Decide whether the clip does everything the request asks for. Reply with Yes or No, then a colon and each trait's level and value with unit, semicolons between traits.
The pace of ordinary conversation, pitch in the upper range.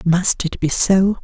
No: average, 195 wpm; medium, 180 Hz